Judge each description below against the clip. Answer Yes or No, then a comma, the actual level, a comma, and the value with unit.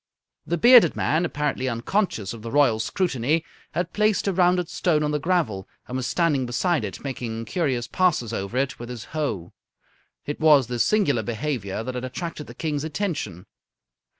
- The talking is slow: No, average, 175 wpm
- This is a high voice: No, medium, 145 Hz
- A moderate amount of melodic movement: No, wide, 6.2 semitones